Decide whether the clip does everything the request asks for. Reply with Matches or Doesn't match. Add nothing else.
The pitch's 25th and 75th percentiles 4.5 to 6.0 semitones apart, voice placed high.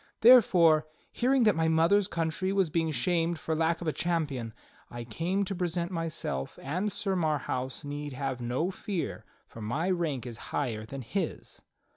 Doesn't match